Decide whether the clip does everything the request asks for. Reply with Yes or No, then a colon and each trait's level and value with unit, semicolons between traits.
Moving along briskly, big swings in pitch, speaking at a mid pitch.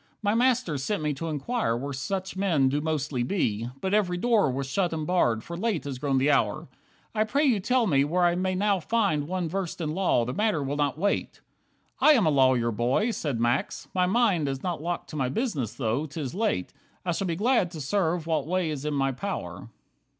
Yes: fast, 220 wpm; wide, 6.2 semitones; medium, 160 Hz